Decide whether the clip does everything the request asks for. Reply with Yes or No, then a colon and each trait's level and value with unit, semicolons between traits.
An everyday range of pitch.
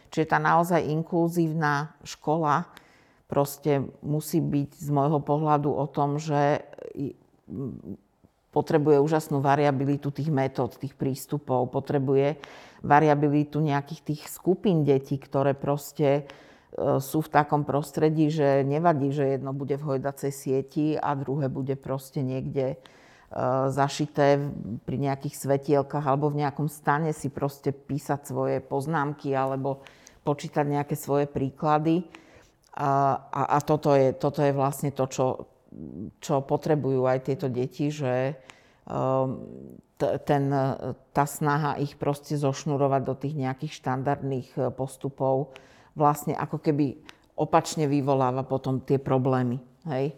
No: narrow, 1.7 semitones